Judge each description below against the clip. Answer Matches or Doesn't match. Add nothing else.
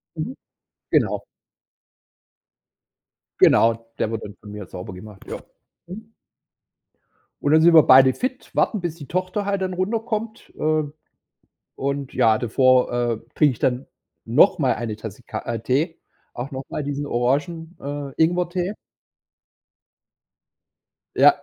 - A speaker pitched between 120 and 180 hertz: Matches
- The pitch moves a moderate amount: Doesn't match